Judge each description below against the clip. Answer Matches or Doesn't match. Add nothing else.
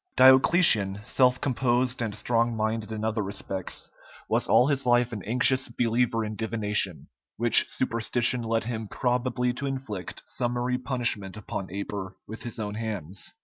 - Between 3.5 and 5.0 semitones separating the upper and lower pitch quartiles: Doesn't match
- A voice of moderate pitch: Doesn't match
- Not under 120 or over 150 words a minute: Matches